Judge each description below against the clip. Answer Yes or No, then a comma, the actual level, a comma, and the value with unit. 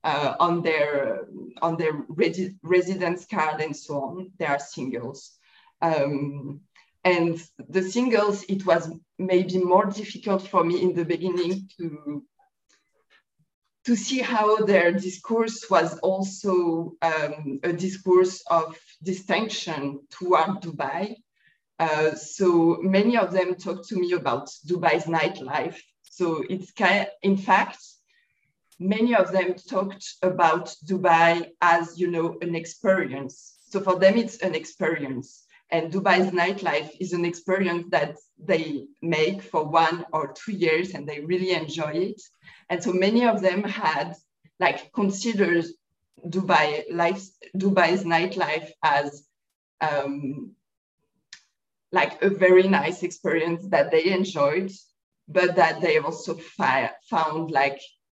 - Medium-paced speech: No, slow, 130 wpm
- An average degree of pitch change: Yes, average, 3.3 semitones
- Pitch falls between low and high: Yes, medium, 175 Hz